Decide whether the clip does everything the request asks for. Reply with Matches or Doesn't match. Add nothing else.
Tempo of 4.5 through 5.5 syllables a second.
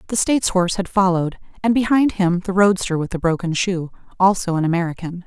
Doesn't match